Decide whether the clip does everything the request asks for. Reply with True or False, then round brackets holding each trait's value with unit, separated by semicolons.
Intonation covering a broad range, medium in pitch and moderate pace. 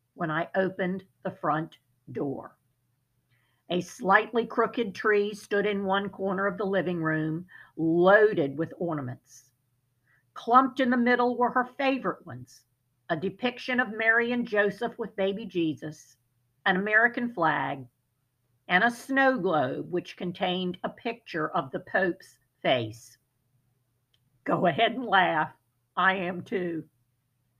False (8.9 semitones; 175 Hz; 130 wpm)